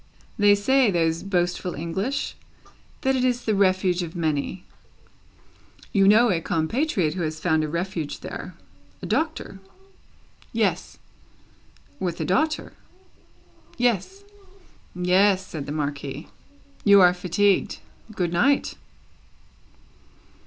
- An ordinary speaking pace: No, slow, 110 wpm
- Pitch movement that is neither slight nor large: Yes, average, 3.7 semitones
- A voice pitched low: No, medium, 185 Hz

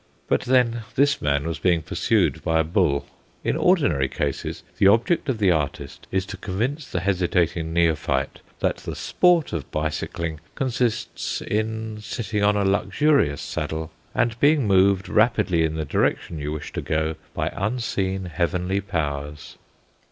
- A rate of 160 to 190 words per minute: No, average, 150 wpm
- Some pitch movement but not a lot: No, wide, 5.8 semitones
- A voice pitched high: No, very low, 95 Hz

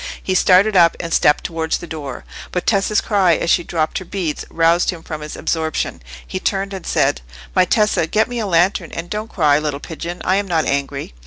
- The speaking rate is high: Yes, fast, 215 wpm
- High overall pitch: No, medium, 170 Hz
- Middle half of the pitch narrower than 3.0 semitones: No, average, 3.3 semitones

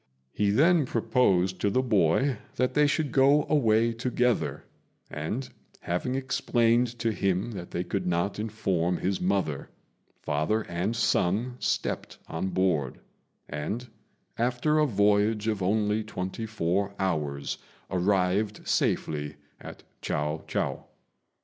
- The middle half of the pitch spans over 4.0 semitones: Yes, average, 4.8 semitones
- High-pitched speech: No, low, 105 Hz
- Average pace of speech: No, slow, 125 wpm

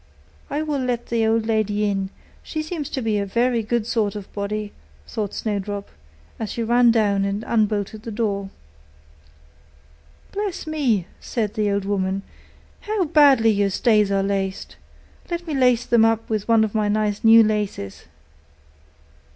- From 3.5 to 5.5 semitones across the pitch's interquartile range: No, average, 2.7 semitones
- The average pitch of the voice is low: No, high, 215 Hz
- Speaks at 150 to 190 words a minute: Yes, average, 160 wpm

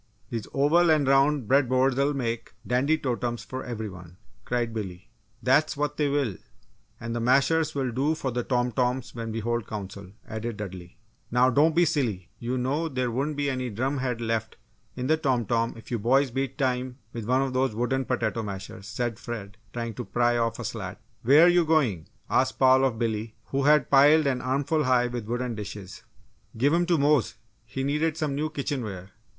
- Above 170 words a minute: Yes, average, 195 wpm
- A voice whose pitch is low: Yes, low, 125 Hz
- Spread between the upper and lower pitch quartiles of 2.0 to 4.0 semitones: Yes, average, 3.5 semitones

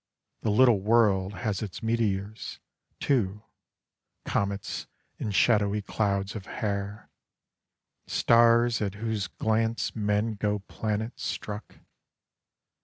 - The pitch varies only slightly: Yes, narrow, 2.1 semitones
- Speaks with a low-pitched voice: Yes, low, 105 Hz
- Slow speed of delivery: Yes, slow, 100 wpm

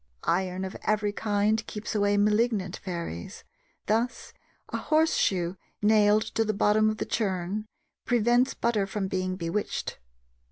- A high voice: Yes, high, 210 Hz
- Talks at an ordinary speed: No, slow, 130 wpm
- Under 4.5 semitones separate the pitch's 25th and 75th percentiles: Yes, narrow, 2.5 semitones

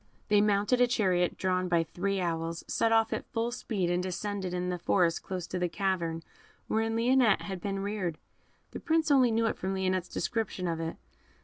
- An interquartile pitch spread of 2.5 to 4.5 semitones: Yes, average, 3.9 semitones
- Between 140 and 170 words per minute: No, average, 195 wpm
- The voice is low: No, high, 190 Hz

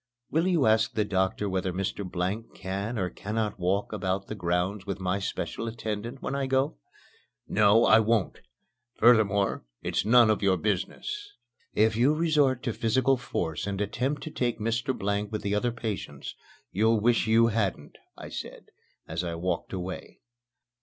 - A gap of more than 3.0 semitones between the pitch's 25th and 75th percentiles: Yes, average, 3.5 semitones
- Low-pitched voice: Yes, low, 105 Hz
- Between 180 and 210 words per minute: No, average, 165 wpm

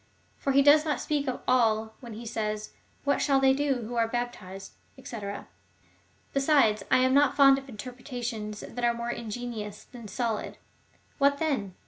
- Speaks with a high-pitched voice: Yes, high, 245 Hz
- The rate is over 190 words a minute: No, average, 165 wpm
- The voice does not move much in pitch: No, average, 3.7 semitones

